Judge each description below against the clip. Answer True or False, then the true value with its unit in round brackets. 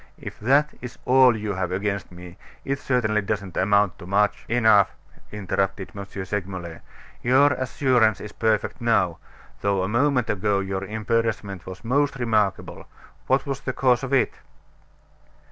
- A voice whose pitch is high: False (105 Hz)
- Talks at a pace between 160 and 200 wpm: False (150 wpm)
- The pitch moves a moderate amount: True (4.2 semitones)